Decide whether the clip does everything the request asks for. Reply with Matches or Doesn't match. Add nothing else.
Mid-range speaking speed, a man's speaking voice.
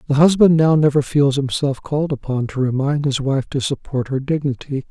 Matches